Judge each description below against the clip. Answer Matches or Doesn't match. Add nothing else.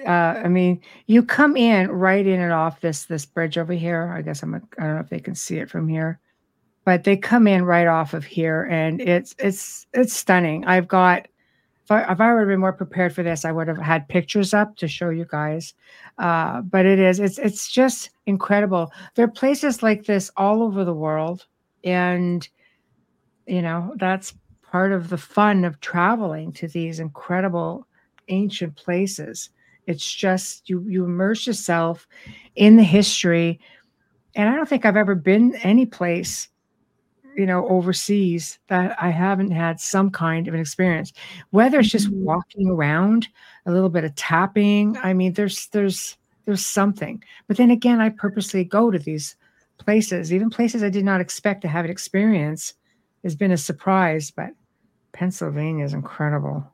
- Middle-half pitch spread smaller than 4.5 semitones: Matches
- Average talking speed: Matches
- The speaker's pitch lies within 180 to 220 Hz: Matches